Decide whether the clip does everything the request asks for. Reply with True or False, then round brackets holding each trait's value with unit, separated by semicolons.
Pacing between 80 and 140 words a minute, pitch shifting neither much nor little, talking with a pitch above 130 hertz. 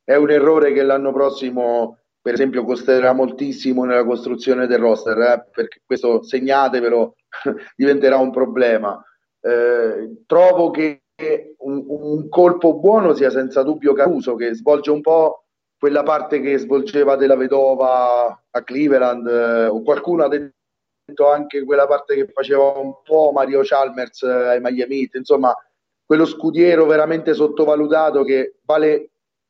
True (135 wpm; 3.0 semitones; 140 Hz)